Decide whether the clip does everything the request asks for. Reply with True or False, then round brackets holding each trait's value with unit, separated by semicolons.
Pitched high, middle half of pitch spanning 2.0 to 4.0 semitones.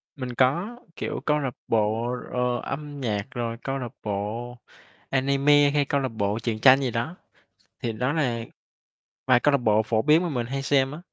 False (130 Hz; 3.5 semitones)